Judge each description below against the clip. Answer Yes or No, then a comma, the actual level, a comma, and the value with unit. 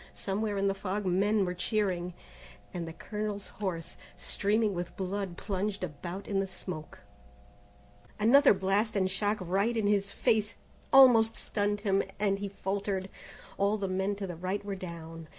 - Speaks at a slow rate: No, average, 160 wpm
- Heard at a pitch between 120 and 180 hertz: No, high, 195 Hz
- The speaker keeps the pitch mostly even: Yes, narrow, 2.0 semitones